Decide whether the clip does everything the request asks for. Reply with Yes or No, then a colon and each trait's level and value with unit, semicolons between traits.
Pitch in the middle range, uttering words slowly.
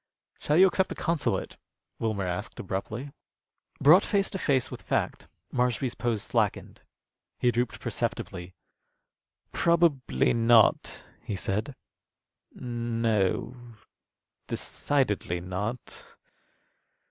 No: low, 120 Hz; slow, 95 wpm